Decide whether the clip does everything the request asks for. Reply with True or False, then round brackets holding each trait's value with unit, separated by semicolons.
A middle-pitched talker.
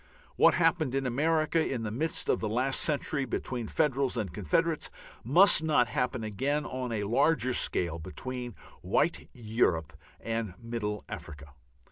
False (125 Hz)